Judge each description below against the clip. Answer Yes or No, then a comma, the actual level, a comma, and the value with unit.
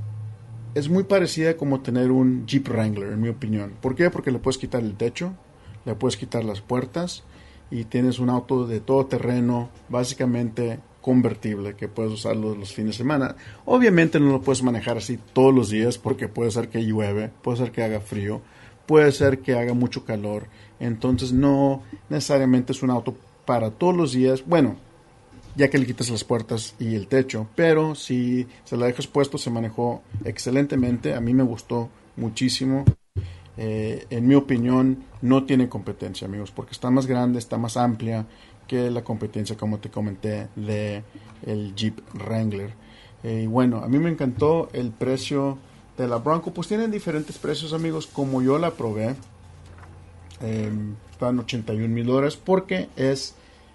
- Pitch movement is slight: No, average, 3.3 semitones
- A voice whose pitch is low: Yes, low, 120 Hz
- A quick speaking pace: No, average, 170 wpm